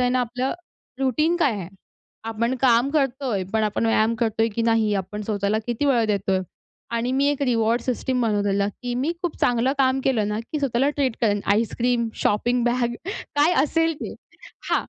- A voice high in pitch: Yes, high, 240 Hz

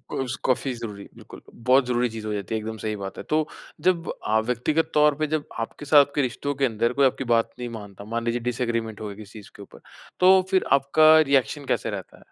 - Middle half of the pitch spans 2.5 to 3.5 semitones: No, average, 4.4 semitones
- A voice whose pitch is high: No, low, 125 Hz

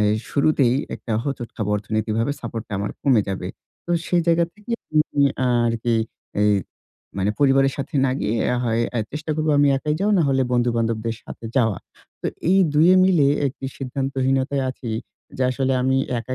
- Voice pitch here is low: Yes, low, 130 Hz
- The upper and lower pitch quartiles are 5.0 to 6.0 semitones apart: No, average, 3.8 semitones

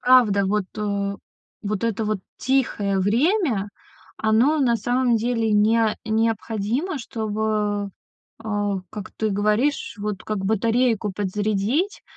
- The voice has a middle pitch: No, high, 215 Hz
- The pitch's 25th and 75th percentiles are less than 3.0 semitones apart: Yes, narrow, 2.5 semitones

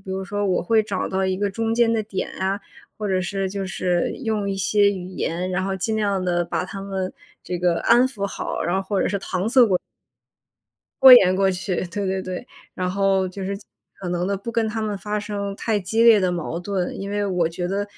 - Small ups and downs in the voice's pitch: Yes, narrow, 1.9 semitones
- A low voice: No, high, 195 Hz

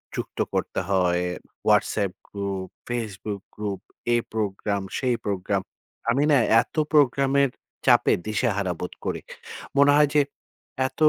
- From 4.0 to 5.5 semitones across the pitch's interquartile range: Yes, average, 5.1 semitones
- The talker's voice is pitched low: Yes, low, 105 Hz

